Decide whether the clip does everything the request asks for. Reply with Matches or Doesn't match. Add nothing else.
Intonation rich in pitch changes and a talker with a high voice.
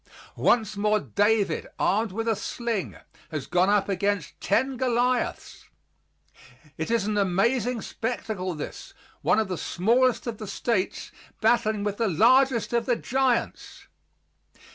Doesn't match